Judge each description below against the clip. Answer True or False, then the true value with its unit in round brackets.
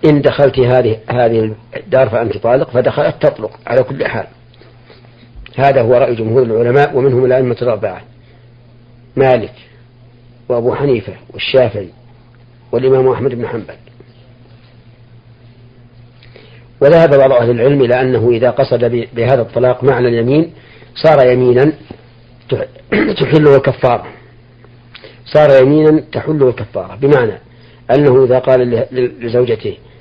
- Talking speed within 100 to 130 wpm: True (105 wpm)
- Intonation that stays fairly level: True (1.6 semitones)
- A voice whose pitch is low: True (120 Hz)